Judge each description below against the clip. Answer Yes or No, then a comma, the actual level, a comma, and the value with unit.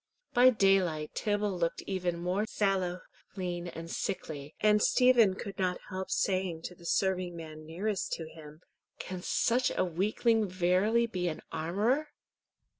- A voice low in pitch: No, medium, 185 Hz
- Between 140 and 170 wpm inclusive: Yes, average, 145 wpm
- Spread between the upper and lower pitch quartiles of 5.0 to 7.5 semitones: No, average, 3.3 semitones